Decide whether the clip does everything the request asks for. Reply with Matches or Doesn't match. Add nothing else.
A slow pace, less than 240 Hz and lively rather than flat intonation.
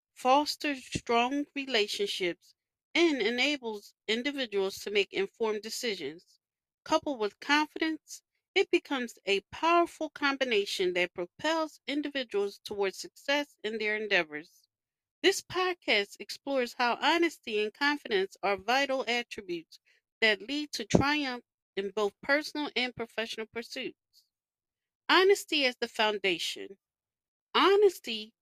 Doesn't match